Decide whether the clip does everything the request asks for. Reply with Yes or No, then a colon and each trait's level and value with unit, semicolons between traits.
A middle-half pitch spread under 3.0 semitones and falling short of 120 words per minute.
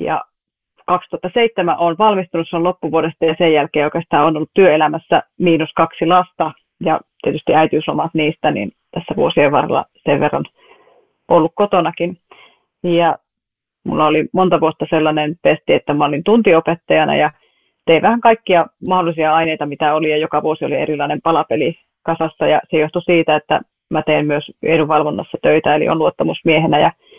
No: narrow, 2.6 semitones; average, 150 wpm